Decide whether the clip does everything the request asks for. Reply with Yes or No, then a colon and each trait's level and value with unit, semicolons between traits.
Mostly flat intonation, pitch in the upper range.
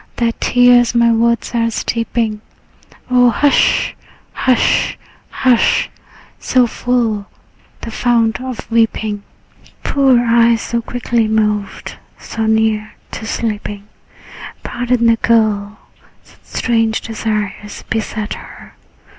Yes: narrow, 1.7 semitones; high, 230 Hz